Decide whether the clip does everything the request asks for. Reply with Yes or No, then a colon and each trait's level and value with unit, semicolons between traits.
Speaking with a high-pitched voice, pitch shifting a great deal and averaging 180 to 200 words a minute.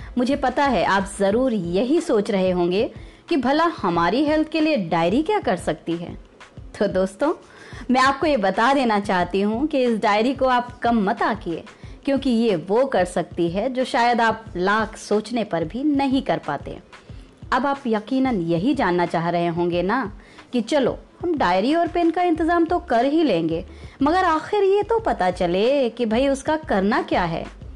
Yes: high, 245 Hz; wide, 7.1 semitones; fast, 190 wpm